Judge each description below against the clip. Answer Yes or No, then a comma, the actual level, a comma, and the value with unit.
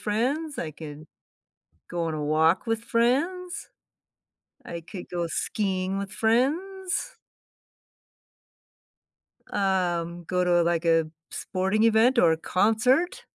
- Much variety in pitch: Yes, wide, 6.1 semitones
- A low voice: No, high, 195 Hz